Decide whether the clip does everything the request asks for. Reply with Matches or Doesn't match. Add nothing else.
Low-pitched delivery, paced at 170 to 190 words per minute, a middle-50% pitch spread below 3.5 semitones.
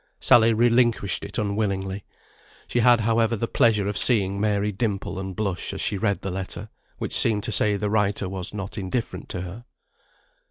Matches